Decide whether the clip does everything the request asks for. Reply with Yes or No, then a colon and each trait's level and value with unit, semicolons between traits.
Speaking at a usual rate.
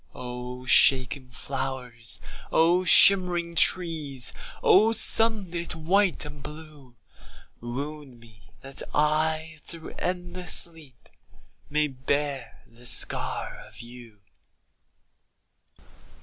No: slow, 90 wpm